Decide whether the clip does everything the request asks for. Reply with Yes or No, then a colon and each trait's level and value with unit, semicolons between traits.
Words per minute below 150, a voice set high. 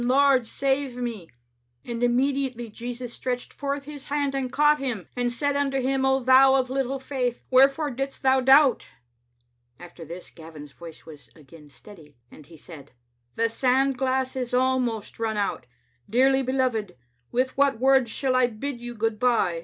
No: average, 170 wpm; very high, 250 Hz